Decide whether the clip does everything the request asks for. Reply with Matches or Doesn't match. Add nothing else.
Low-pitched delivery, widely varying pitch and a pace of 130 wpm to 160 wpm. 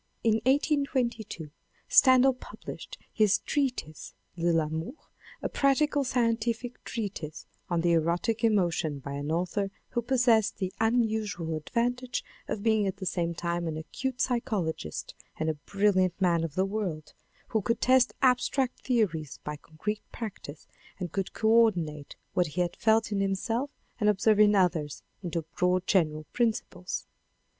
Doesn't match